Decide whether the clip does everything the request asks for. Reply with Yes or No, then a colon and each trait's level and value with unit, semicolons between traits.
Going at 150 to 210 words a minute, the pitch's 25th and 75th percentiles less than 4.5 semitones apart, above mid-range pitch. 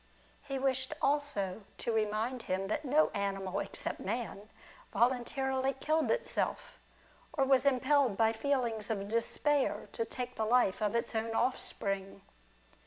No: slow, 135 wpm; average, 4.0 semitones; high, 240 Hz